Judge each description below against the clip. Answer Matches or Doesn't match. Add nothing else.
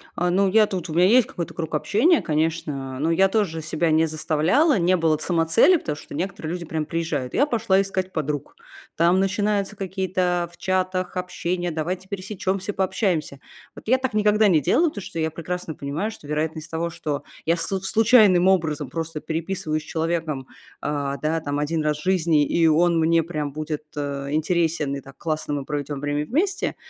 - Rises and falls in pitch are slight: Doesn't match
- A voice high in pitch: Doesn't match